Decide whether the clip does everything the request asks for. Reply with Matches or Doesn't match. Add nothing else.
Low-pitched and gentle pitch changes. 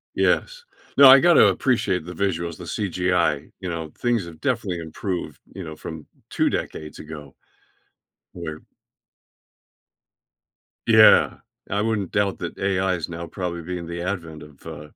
Doesn't match